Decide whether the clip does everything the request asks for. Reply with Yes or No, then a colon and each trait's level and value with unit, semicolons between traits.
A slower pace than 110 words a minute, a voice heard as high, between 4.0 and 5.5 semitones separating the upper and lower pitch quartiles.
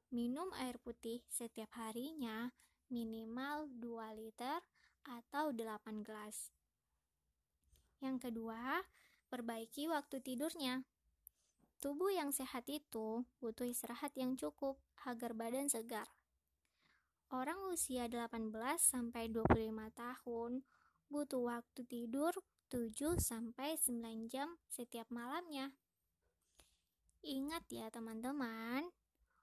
No: average, 90 wpm; high, 245 Hz; average, 3.4 semitones